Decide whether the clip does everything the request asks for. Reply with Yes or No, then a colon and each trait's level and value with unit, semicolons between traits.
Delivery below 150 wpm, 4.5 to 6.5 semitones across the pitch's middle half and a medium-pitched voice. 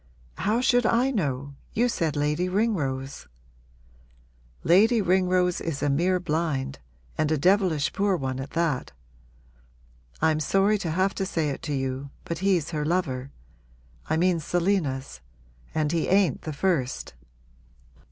Yes: average, 140 wpm; average, 4.9 semitones; medium, 165 Hz